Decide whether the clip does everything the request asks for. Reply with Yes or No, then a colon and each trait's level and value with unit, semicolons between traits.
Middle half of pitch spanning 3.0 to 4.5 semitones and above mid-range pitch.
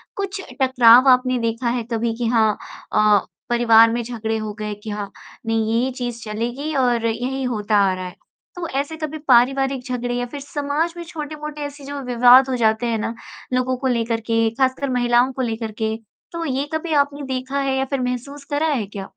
Yes: average, 3.4 semitones; very high, 250 Hz